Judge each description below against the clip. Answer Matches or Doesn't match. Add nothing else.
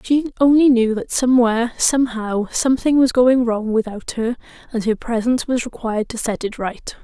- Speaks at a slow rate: Doesn't match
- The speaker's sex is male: Doesn't match